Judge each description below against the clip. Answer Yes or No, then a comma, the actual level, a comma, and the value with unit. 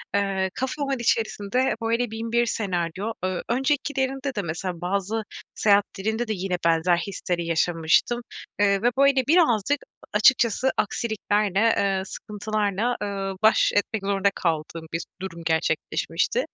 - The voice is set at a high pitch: Yes, high, 205 Hz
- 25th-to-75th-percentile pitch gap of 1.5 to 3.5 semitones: No, average, 4.2 semitones